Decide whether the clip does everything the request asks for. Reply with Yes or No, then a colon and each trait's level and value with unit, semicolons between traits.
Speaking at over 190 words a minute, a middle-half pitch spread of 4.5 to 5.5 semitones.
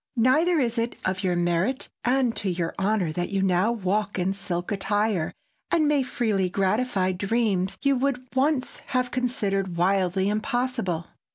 No: average, 155 wpm; average, 5.1 semitones